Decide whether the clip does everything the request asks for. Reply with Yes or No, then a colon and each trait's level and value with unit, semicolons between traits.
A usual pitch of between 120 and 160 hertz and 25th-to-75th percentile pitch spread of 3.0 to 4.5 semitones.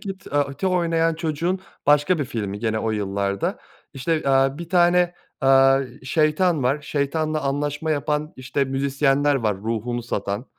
Yes: medium, 140 Hz; average, 4.0 semitones